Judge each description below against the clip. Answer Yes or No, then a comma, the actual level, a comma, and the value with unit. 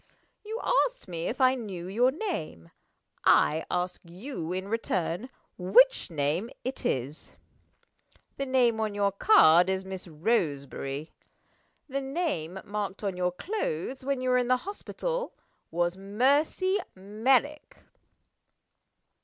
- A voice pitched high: Yes, high, 205 Hz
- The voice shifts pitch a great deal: Yes, wide, 7.1 semitones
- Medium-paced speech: No, slow, 125 wpm